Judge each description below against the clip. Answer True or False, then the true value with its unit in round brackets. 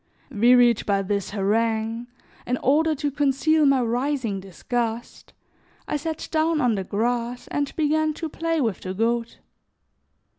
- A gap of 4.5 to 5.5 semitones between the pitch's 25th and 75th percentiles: True (4.9 semitones)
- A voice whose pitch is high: True (245 Hz)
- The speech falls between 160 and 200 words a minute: False (140 wpm)